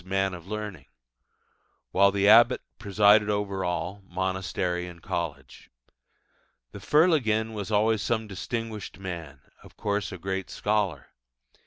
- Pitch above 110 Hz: No, low, 100 Hz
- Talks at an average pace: No, slow, 130 wpm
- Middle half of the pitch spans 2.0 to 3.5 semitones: Yes, average, 2.7 semitones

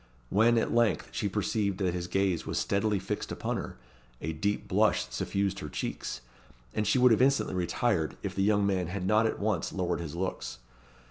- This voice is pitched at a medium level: No, low, 100 Hz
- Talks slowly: No, average, 195 wpm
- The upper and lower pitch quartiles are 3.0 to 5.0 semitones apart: Yes, average, 3.4 semitones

